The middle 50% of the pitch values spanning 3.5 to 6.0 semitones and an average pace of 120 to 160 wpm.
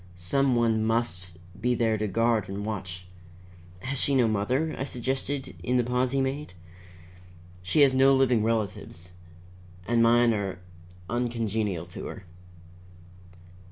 Yes: average, 4.6 semitones; average, 140 wpm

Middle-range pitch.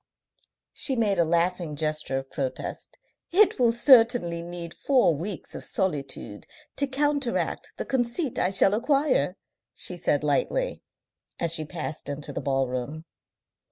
Yes: medium, 175 Hz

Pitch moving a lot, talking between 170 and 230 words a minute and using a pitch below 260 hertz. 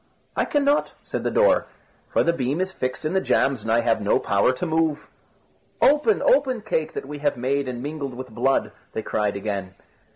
Yes: wide, 7.0 semitones; average, 200 wpm; medium, 140 Hz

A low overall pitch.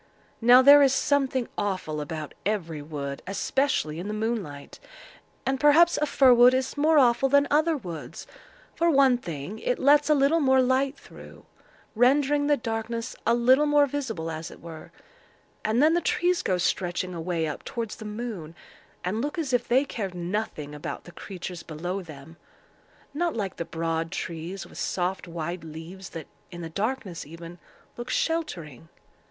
No: high, 220 Hz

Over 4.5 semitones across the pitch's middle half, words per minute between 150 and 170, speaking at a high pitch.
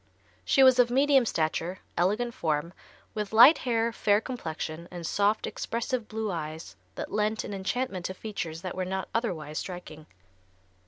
Yes: wide, 5.4 semitones; average, 155 wpm; high, 200 Hz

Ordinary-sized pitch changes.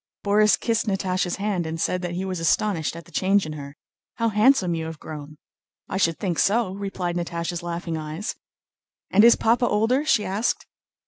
Yes: average, 3.9 semitones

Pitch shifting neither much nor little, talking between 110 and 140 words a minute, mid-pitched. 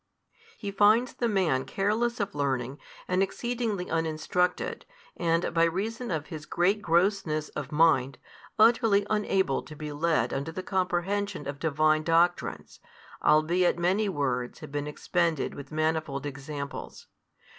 Yes: average, 4.7 semitones; slow, 135 wpm; medium, 165 Hz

